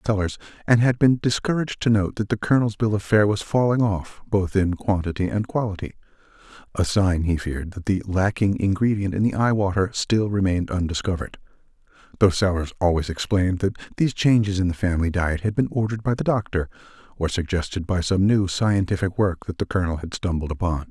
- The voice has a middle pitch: No, low, 100 Hz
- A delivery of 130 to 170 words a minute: No, average, 180 wpm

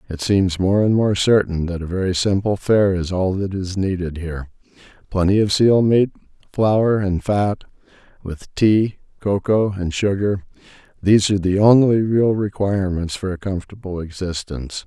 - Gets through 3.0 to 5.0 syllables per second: Yes, 4.8 syllables/s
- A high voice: No, very low, 95 Hz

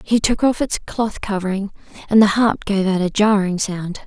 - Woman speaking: Yes, female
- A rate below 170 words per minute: No, fast, 205 wpm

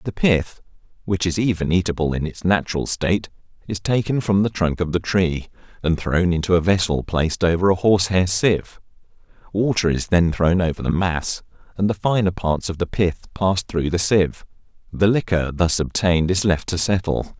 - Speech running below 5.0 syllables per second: No, 5.2 syllables/s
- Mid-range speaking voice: No, very low, 90 Hz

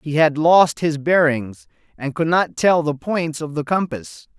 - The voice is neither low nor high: Yes, medium, 155 Hz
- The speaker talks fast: No, average, 190 wpm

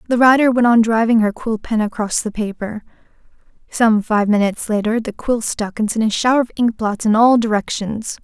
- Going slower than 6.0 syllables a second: Yes, 5.4 syllables/s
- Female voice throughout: Yes, female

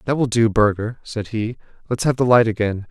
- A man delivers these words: Yes, male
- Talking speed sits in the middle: No, fast, 230 wpm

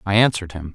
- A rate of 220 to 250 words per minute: Yes, fast, 240 wpm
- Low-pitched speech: Yes, very low, 95 Hz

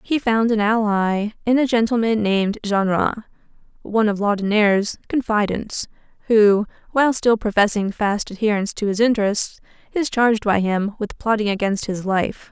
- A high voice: Yes, high, 215 Hz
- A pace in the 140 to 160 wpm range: Yes, average, 150 wpm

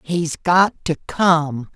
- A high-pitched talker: No, medium, 165 Hz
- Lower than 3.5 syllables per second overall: Yes, 2.6 syllables/s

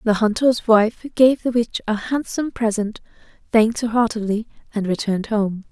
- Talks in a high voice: Yes, high, 225 Hz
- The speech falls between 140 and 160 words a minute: Yes, average, 155 wpm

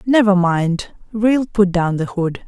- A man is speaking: No, female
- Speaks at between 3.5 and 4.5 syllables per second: Yes, 3.7 syllables/s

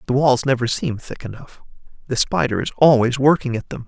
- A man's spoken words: Yes, male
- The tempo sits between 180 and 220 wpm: Yes, average, 200 wpm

